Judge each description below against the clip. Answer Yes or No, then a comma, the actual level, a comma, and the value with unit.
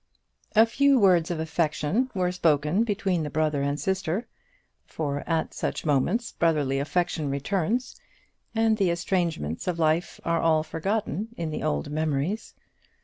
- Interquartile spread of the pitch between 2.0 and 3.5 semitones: No, average, 4.3 semitones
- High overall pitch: No, medium, 165 Hz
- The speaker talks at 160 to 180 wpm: No, average, 145 wpm